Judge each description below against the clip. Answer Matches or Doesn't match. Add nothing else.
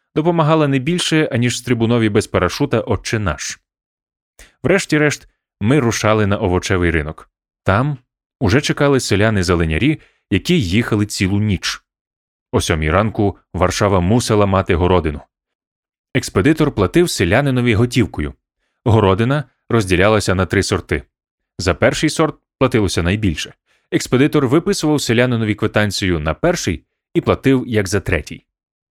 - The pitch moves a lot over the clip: Matches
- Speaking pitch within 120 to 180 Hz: Doesn't match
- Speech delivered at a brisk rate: Doesn't match